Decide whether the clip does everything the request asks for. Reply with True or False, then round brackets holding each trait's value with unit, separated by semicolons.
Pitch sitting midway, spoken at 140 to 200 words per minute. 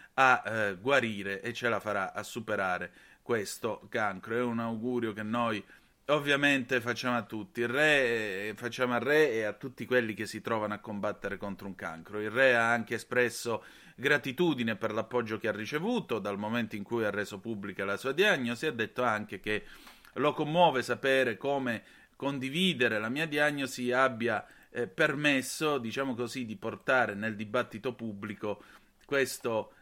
False (120 Hz; 165 wpm)